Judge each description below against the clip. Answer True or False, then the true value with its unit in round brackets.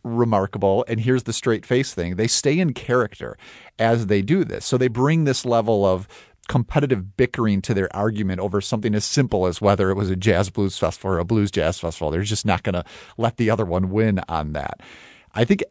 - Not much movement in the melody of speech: False (3.8 semitones)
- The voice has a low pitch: True (105 Hz)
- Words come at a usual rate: False (220 wpm)